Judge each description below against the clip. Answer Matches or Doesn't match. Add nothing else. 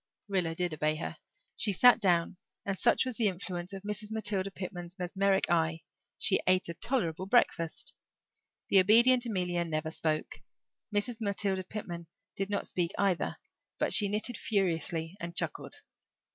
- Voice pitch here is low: Doesn't match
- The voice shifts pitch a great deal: Doesn't match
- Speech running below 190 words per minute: Matches